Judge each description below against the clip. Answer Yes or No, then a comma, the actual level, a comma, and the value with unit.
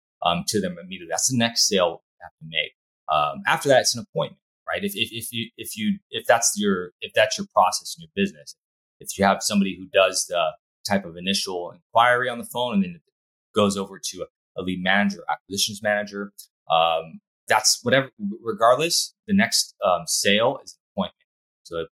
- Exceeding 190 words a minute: Yes, average, 200 wpm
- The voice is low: Yes, low, 115 Hz